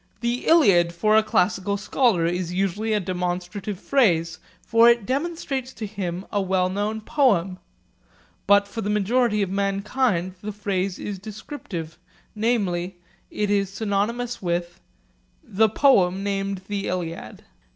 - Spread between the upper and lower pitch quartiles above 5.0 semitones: No, average, 3.3 semitones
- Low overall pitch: No, high, 200 Hz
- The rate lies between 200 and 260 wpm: No, slow, 135 wpm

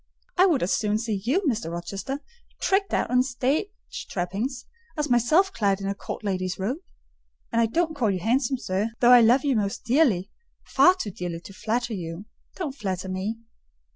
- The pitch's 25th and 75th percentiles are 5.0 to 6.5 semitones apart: Yes, wide, 5.6 semitones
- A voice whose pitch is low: No, high, 230 Hz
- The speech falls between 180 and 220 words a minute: Yes, average, 185 wpm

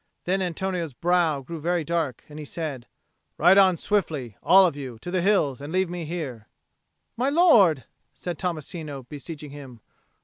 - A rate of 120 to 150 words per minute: No, average, 160 wpm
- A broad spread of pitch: No, average, 4.0 semitones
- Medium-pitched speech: Yes, medium, 165 Hz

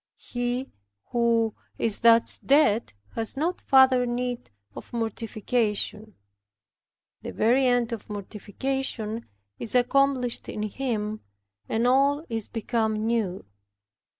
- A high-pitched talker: Yes, high, 235 Hz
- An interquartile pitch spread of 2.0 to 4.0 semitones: Yes, narrow, 2.6 semitones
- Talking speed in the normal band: No, slow, 105 wpm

